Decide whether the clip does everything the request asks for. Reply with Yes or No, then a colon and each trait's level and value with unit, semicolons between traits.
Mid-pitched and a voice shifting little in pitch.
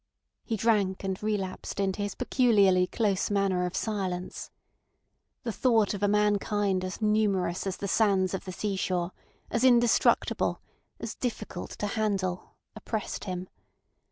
No: high, 200 Hz; narrow, 2.3 semitones